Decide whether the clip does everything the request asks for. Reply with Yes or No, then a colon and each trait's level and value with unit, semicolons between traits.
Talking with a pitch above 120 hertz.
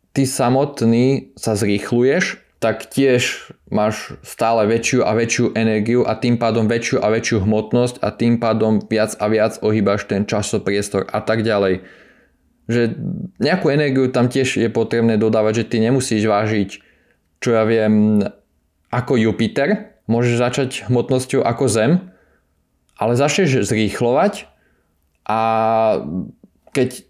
No: low, 115 Hz